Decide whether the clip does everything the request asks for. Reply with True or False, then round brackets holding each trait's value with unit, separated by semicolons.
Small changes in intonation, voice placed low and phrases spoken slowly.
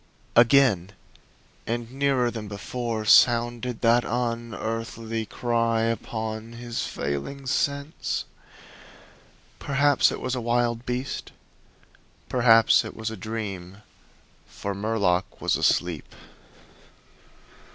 True (1.9 semitones; 115 Hz; 95 wpm)